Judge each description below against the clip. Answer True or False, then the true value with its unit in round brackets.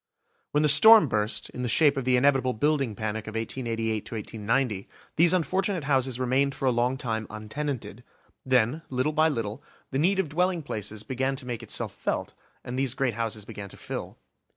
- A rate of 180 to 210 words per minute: True (190 wpm)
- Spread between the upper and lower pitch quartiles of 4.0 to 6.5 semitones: True (4.5 semitones)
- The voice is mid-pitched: False (130 Hz)